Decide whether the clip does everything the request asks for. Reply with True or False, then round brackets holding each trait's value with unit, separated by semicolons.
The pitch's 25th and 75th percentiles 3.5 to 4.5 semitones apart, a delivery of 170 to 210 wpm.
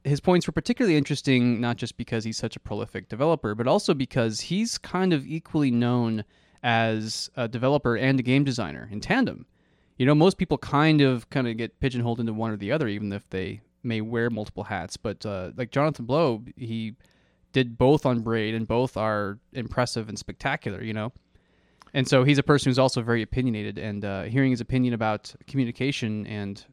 True (3.8 semitones; 195 wpm)